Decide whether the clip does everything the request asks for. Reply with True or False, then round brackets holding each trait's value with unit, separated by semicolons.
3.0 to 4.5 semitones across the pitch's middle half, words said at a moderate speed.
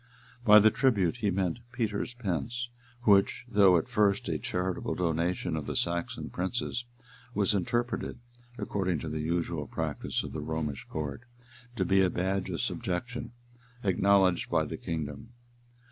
True (3.8 semitones; 145 wpm)